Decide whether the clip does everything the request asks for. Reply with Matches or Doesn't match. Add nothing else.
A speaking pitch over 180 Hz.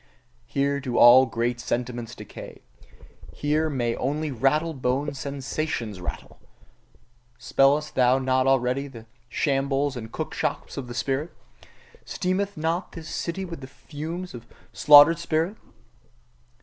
Doesn't match